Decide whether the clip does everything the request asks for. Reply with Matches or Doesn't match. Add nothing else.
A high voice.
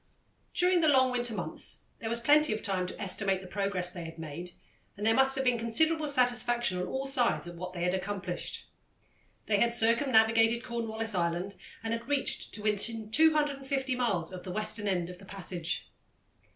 Matches